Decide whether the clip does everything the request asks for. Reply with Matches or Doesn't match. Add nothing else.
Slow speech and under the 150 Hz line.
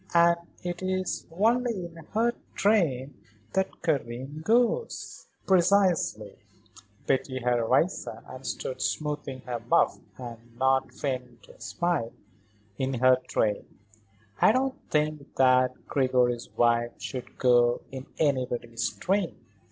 Matches